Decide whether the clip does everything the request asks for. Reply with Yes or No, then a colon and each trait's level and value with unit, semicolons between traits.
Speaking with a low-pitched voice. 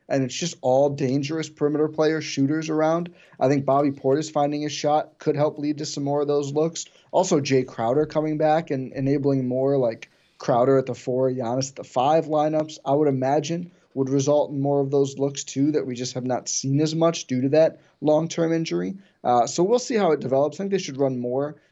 No: medium, 145 Hz